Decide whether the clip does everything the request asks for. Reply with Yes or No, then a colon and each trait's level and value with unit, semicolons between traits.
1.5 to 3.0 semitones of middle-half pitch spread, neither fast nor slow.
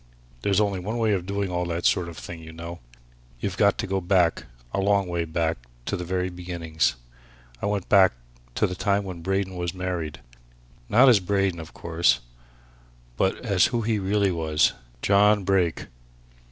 Yes: average, 2.7 semitones; average, 180 wpm